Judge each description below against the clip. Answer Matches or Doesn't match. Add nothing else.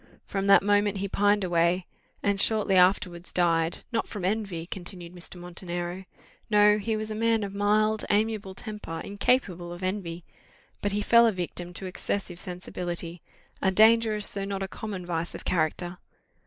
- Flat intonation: Doesn't match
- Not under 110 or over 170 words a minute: Matches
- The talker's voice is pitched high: Matches